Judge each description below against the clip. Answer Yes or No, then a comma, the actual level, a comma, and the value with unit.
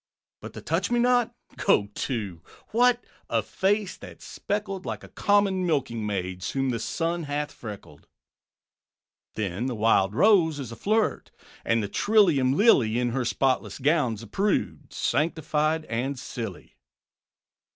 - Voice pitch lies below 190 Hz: Yes, medium, 140 Hz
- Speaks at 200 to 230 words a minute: No, average, 140 wpm